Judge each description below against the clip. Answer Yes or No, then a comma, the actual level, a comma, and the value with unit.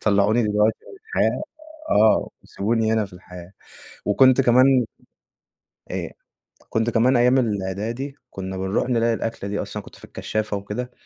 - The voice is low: Yes, low, 110 Hz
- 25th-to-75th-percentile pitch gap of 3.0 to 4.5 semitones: Yes, average, 3.4 semitones